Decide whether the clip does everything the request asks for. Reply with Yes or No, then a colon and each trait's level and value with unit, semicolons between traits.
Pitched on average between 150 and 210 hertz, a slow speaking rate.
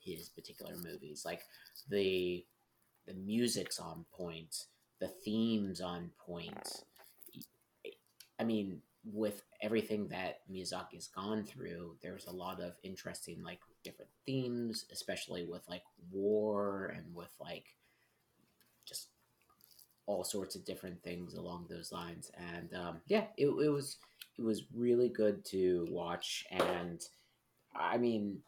No: low, 100 Hz; slow, 125 wpm